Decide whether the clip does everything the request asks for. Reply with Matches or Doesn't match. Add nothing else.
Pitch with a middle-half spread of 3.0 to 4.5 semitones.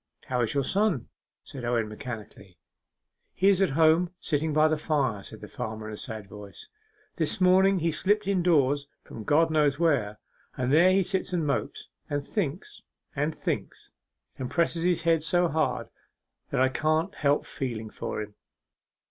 Doesn't match